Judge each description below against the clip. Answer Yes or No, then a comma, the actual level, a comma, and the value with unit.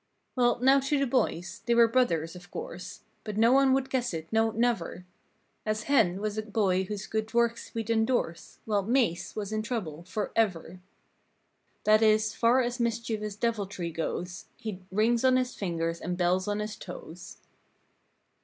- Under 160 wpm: No, average, 165 wpm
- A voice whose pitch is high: Yes, high, 215 Hz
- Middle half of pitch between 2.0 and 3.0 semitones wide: No, average, 4.3 semitones